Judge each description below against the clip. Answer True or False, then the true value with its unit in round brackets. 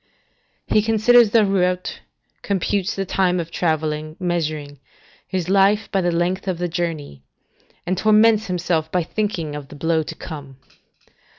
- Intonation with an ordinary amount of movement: True (3.7 semitones)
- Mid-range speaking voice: True (180 Hz)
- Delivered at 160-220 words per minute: False (150 wpm)